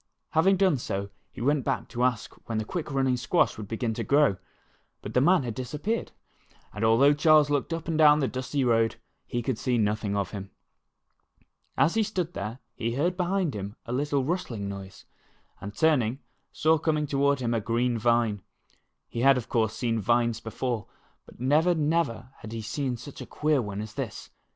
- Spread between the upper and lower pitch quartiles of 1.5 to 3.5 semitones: No, average, 5.0 semitones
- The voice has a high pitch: No, low, 125 Hz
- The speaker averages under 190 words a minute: No, average, 195 wpm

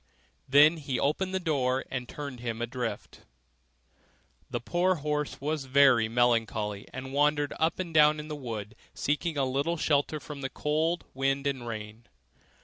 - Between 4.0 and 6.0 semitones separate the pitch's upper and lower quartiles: No, average, 3.6 semitones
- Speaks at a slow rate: No, average, 155 wpm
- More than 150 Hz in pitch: No, medium, 140 Hz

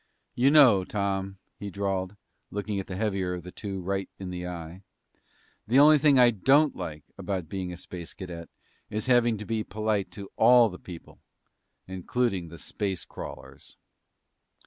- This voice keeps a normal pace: Yes, average, 160 wpm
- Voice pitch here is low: Yes, low, 100 Hz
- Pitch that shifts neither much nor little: Yes, average, 3.6 semitones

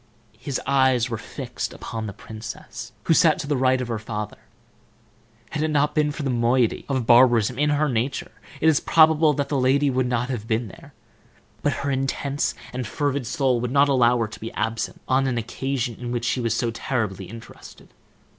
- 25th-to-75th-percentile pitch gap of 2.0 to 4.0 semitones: Yes, average, 3.3 semitones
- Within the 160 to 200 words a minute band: Yes, average, 195 wpm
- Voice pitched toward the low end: Yes, low, 130 Hz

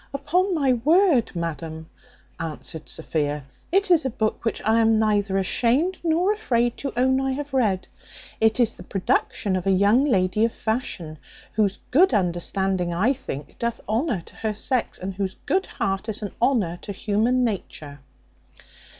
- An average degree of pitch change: No, wide, 5.7 semitones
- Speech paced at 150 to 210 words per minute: Yes, average, 165 wpm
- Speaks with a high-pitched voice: Yes, high, 220 Hz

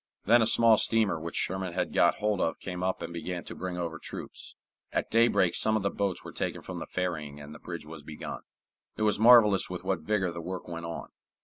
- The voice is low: Yes, very low, 90 Hz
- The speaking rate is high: Yes, fast, 230 wpm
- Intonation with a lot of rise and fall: No, average, 4.0 semitones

